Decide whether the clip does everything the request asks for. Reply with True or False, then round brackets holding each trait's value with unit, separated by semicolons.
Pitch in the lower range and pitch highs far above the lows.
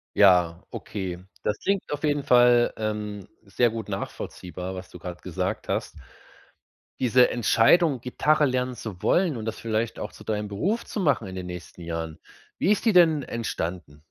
True (110 Hz; 5.8 semitones)